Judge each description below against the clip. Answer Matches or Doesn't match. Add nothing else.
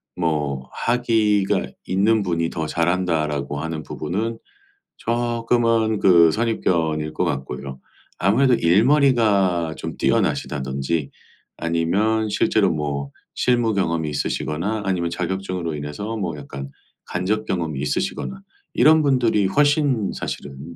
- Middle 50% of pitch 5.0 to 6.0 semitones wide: Doesn't match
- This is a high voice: Doesn't match